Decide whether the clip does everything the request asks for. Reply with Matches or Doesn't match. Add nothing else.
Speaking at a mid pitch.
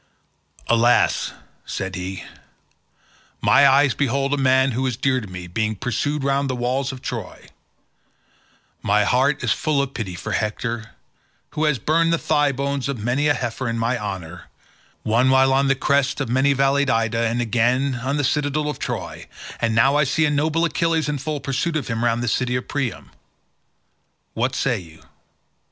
Doesn't match